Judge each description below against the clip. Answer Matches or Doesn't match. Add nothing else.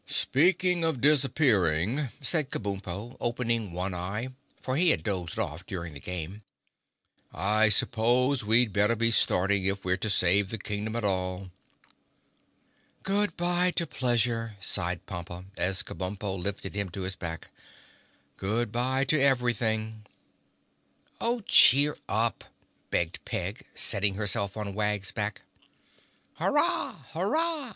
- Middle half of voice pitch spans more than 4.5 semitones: Matches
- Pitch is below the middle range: Matches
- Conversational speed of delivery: Doesn't match